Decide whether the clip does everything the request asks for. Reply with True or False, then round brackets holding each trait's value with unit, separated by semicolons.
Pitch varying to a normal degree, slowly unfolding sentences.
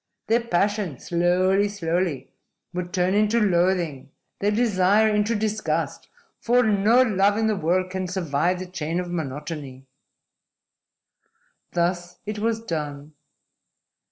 True (3.5 semitones; 120 wpm)